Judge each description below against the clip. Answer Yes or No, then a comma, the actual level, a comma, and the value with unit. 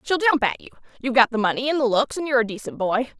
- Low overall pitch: No, very high, 250 Hz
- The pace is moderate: No, fast, 300 wpm